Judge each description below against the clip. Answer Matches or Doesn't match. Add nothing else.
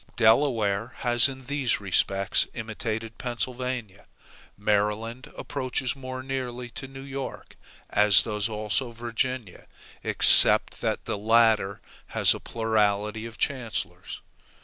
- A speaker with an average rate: Doesn't match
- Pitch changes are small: Doesn't match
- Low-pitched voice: Matches